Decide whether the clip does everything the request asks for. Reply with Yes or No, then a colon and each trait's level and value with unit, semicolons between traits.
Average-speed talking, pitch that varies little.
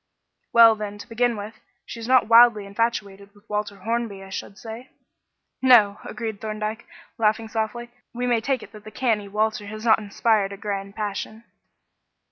Yes: average, 170 wpm; narrow, 2.1 semitones